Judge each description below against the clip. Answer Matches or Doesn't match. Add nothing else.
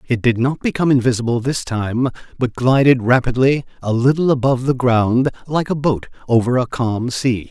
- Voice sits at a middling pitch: Doesn't match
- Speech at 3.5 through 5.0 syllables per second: Doesn't match